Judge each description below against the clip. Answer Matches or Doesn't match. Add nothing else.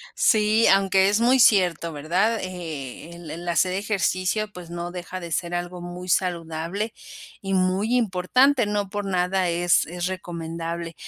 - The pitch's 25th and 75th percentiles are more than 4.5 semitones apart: Doesn't match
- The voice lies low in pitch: Doesn't match